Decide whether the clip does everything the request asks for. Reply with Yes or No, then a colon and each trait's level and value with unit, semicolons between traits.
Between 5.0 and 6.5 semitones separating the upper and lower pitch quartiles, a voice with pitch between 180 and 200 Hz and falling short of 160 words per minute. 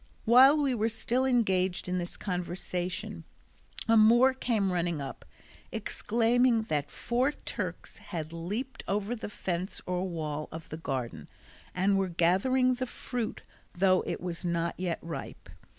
Yes: wide, 5.5 semitones; high, 190 Hz; average, 145 wpm